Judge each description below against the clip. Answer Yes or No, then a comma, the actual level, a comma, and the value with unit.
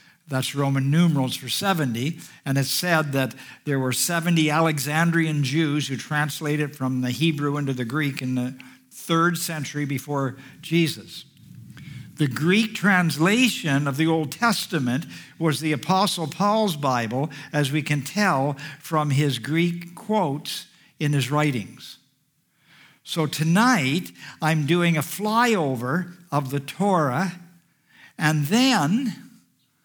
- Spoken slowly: Yes, slow, 125 wpm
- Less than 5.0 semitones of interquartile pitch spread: Yes, average, 3.8 semitones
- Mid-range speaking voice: Yes, medium, 155 Hz